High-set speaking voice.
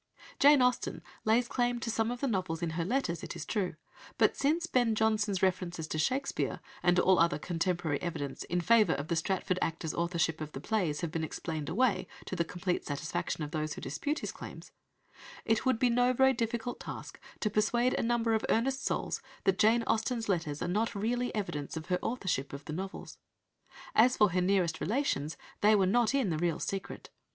Yes: high, 195 Hz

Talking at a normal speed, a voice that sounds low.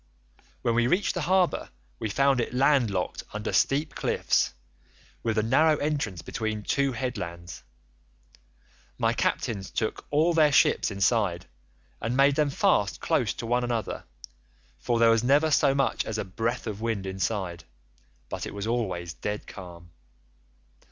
Yes: average, 155 wpm; low, 115 Hz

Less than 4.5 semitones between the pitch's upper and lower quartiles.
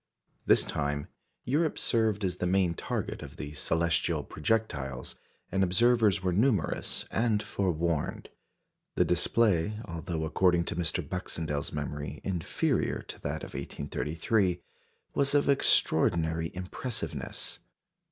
No: average, 5.0 semitones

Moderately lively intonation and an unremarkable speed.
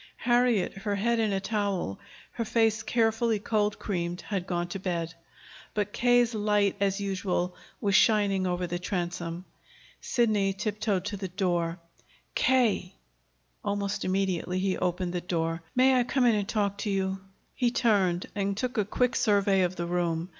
Yes: average, 3.2 semitones; average, 160 wpm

